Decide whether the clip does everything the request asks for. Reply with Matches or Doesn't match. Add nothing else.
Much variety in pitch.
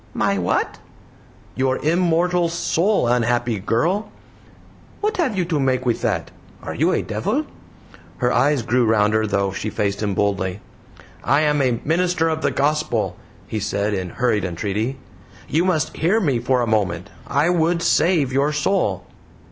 Matches